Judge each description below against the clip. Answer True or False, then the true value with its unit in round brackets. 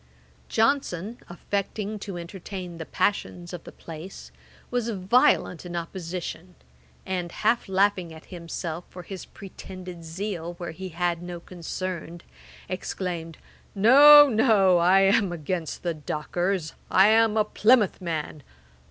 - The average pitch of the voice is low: False (185 Hz)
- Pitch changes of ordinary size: True (3.0 semitones)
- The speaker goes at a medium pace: False (125 wpm)